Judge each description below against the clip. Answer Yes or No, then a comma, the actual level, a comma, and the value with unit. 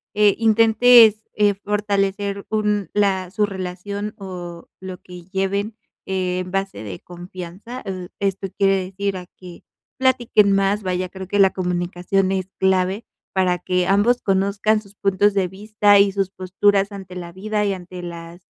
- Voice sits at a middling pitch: No, high, 195 Hz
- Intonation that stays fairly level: Yes, narrow, 2.0 semitones